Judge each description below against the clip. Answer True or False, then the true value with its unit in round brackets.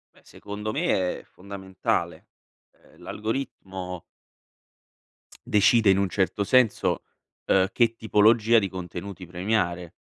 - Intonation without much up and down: False (3.0 semitones)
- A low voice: True (100 Hz)